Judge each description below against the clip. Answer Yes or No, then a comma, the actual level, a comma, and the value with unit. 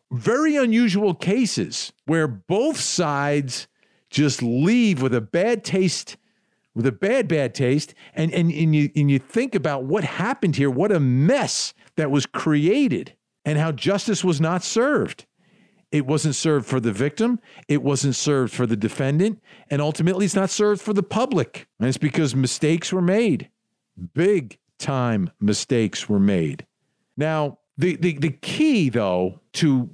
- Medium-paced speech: Yes, average, 155 wpm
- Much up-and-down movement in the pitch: Yes, wide, 6.4 semitones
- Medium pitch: Yes, medium, 155 Hz